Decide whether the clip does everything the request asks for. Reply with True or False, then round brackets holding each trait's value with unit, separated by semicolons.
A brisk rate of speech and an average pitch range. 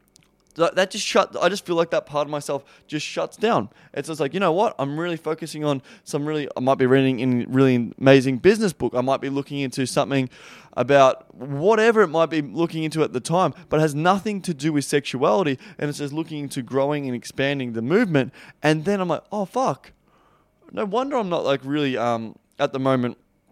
True (215 wpm; 4.0 semitones)